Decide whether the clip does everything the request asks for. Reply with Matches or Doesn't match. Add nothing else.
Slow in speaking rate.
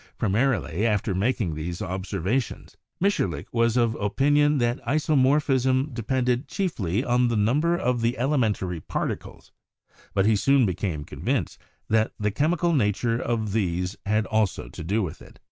Doesn't match